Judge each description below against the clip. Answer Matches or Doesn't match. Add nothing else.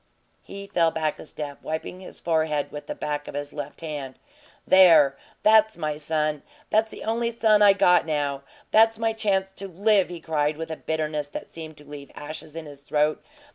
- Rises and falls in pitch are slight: Doesn't match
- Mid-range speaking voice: Matches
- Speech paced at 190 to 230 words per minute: Matches